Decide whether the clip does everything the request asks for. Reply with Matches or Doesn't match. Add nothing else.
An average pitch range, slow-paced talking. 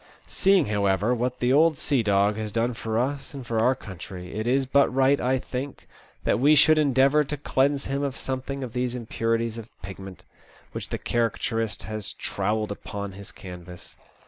Doesn't match